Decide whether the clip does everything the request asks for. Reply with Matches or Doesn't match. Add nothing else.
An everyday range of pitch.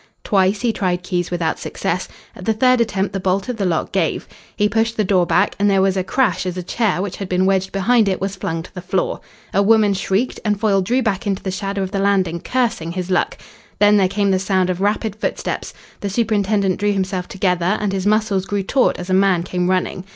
Doesn't match